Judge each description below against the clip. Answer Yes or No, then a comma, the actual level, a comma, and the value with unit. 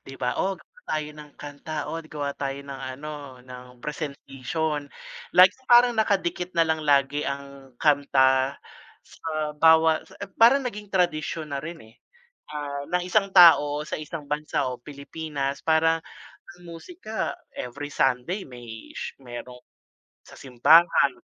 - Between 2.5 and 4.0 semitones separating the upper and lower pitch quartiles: Yes, average, 3.1 semitones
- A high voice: No, medium, 150 Hz